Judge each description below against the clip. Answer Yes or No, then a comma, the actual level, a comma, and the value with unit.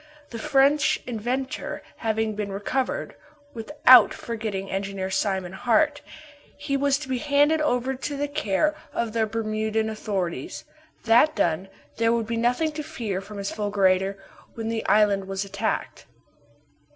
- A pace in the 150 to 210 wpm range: No, average, 140 wpm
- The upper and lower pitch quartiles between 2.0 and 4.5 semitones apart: No, average, 5.1 semitones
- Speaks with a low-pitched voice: No, high, 225 Hz